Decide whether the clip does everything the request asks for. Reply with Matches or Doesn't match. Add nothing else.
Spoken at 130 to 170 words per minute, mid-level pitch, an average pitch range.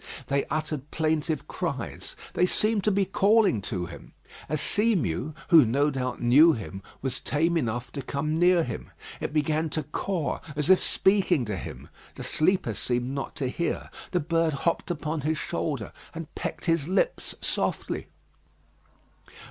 Matches